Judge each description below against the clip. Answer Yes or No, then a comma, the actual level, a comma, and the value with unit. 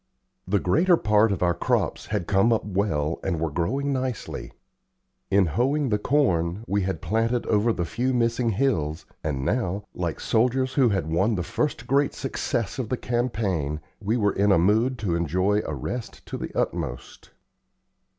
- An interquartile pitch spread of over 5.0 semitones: Yes, wide, 5.5 semitones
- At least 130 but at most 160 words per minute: No, average, 170 wpm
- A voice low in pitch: Yes, low, 105 Hz